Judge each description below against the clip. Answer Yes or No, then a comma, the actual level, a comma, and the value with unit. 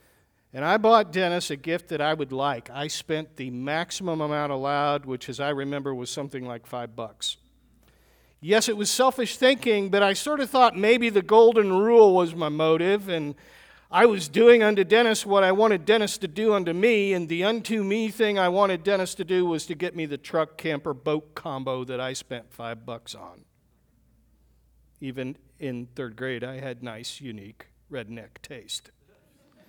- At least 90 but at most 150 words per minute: No, average, 185 wpm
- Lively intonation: Yes, wide, 7.6 semitones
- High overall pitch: No, medium, 160 Hz